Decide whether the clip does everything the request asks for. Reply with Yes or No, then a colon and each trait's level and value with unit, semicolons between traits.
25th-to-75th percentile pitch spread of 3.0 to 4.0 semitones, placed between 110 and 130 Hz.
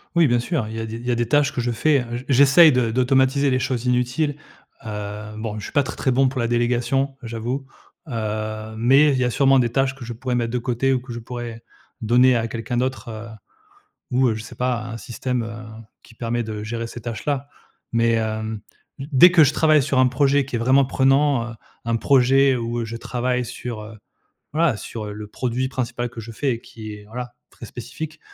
No: narrow, 2.6 semitones; low, 120 Hz